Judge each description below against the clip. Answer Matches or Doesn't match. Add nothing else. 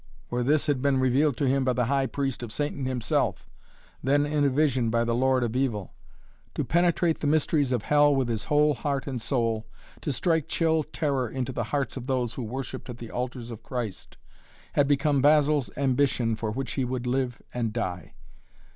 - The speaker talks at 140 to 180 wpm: Doesn't match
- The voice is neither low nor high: Doesn't match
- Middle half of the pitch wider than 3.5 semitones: Doesn't match